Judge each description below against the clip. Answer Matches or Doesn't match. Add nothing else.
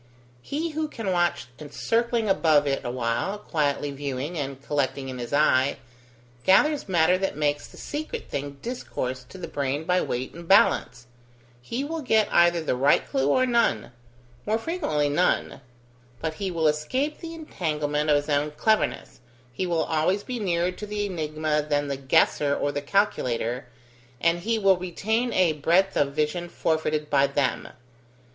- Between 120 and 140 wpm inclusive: Doesn't match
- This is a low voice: Doesn't match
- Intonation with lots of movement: Matches